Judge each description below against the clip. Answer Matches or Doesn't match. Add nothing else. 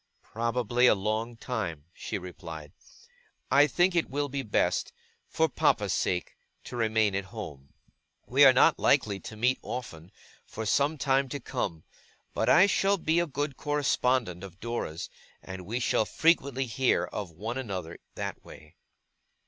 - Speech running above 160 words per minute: Doesn't match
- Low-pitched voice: Matches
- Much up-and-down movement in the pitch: Matches